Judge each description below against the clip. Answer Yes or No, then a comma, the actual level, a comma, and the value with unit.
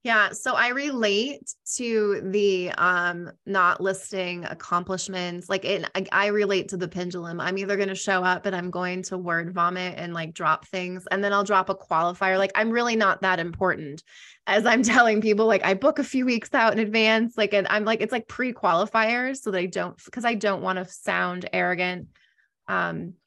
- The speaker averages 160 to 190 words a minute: No, average, 200 wpm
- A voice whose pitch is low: No, high, 195 Hz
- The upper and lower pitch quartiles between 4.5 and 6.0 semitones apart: No, average, 3.4 semitones